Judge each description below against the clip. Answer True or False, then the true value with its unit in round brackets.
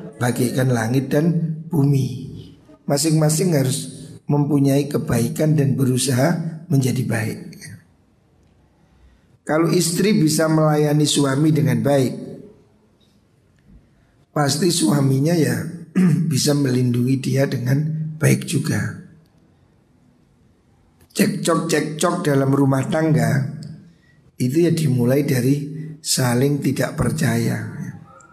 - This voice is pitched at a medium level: True (145 Hz)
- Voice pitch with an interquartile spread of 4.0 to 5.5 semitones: False (2.8 semitones)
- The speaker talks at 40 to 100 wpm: True (85 wpm)